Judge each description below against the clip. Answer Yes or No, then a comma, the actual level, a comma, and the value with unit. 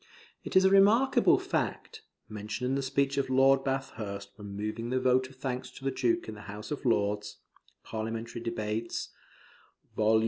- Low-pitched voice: Yes, low, 125 Hz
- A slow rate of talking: No, average, 170 wpm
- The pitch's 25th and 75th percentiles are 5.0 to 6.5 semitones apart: No, average, 3.9 semitones